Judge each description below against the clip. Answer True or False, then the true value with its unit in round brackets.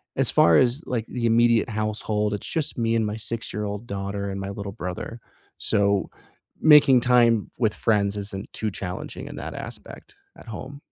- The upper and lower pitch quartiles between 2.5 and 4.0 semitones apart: True (2.8 semitones)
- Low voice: True (110 Hz)